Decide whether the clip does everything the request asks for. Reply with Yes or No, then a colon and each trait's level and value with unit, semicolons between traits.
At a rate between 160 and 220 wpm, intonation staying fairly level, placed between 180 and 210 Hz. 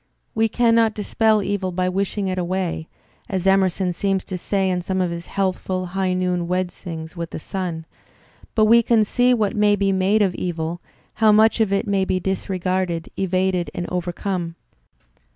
Yes: average, 170 wpm; narrow, 2.2 semitones; high, 190 Hz